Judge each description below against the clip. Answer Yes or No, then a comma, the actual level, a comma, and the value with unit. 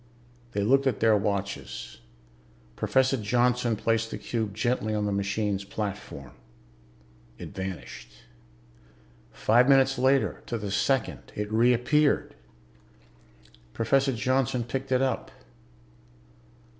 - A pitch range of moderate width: Yes, average, 4.2 semitones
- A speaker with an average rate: No, slow, 105 wpm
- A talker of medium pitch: No, low, 115 Hz